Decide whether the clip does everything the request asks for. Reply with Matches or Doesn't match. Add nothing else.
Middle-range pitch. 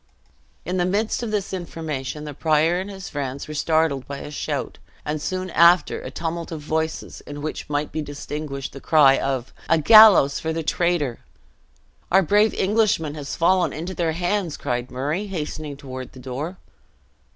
Matches